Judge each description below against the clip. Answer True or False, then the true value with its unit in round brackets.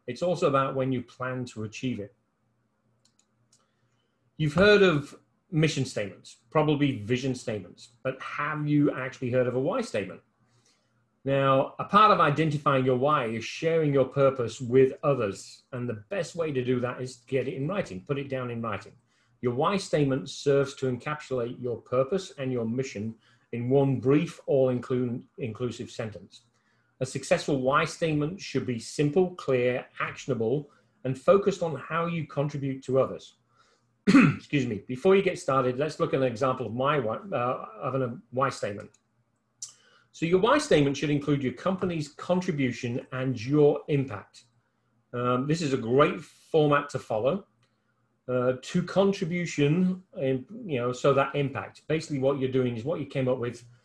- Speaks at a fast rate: False (165 wpm)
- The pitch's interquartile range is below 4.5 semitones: True (3.5 semitones)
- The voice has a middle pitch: False (130 Hz)